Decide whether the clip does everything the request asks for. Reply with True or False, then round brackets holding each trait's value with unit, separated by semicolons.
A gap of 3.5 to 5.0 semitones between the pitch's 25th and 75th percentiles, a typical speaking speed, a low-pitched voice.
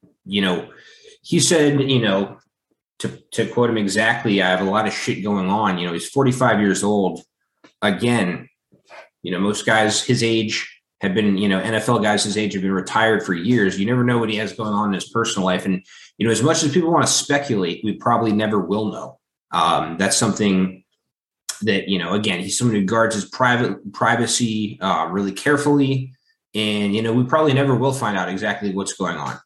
False (4.0 semitones; 210 wpm; 110 Hz)